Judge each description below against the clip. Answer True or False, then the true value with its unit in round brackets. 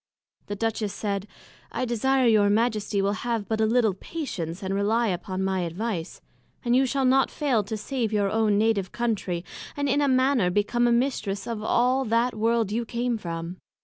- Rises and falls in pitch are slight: False (3.3 semitones)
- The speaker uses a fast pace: False (185 wpm)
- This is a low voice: False (220 Hz)